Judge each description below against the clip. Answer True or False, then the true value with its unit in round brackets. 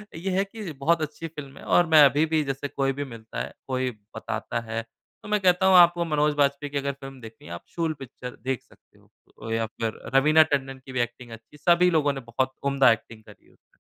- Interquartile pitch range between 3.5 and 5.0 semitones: True (3.8 semitones)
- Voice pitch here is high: False (140 Hz)